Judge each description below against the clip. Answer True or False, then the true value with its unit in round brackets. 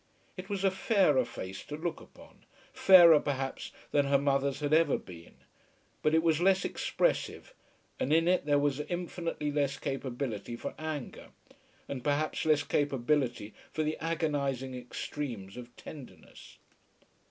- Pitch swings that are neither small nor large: True (3.3 semitones)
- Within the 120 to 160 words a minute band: True (140 wpm)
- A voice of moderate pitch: True (145 Hz)